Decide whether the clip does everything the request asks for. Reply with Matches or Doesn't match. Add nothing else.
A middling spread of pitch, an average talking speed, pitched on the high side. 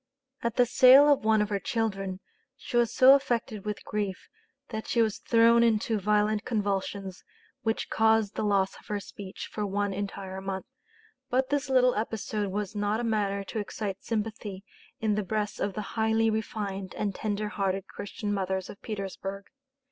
Doesn't match